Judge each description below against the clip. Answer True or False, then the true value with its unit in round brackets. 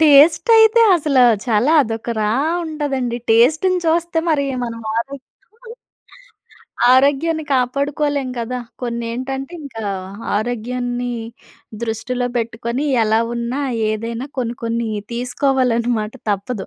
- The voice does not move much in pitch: False (3.5 semitones)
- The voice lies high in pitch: True (250 Hz)